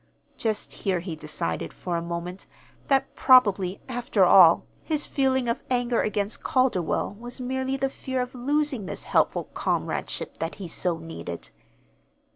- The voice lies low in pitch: No, high, 220 Hz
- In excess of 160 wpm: No, average, 145 wpm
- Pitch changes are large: Yes, wide, 6.7 semitones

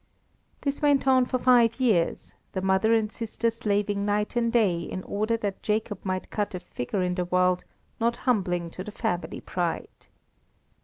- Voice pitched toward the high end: Yes, high, 205 Hz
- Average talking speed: Yes, average, 170 wpm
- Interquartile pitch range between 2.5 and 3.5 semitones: No, average, 4.0 semitones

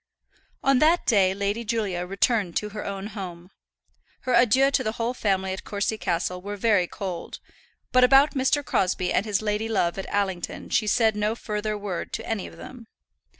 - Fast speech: No, average, 185 wpm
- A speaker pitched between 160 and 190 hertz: No, high, 210 Hz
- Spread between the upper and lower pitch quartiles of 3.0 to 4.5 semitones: Yes, average, 3.4 semitones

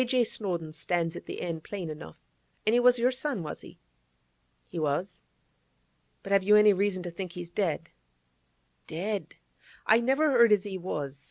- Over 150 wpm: Yes, average, 175 wpm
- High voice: Yes, high, 195 Hz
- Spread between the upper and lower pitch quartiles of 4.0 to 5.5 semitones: Yes, average, 4.7 semitones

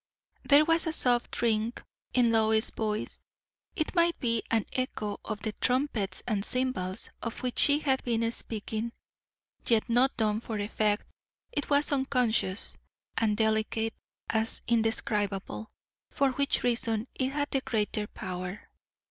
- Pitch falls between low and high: No, high, 230 Hz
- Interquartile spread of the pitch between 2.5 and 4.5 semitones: Yes, average, 3.2 semitones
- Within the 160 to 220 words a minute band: No, average, 140 wpm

